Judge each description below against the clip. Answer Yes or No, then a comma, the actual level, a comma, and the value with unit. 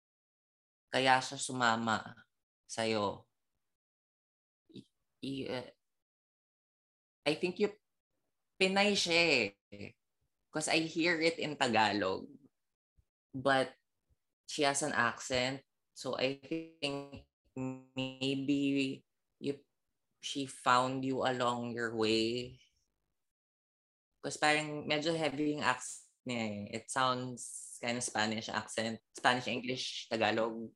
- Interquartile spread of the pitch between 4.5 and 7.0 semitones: No, average, 4.0 semitones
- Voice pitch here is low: Yes, low, 130 Hz